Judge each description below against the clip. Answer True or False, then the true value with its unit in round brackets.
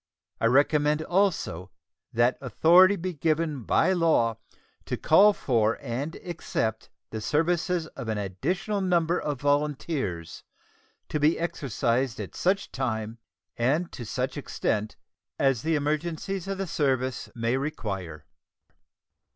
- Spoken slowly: True (125 wpm)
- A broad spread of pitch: True (6.3 semitones)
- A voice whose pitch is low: False (145 Hz)